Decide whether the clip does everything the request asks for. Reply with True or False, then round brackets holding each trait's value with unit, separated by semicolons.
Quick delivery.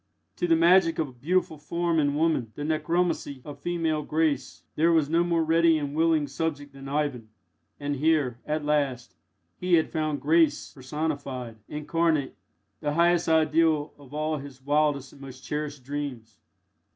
False (160 wpm)